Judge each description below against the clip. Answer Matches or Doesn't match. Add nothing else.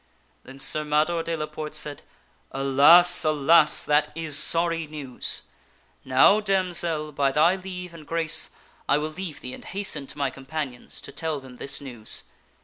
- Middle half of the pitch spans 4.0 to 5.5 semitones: Doesn't match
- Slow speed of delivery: Doesn't match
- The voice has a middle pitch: Matches